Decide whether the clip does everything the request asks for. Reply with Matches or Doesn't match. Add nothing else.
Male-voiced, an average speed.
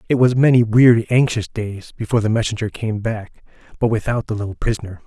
Matches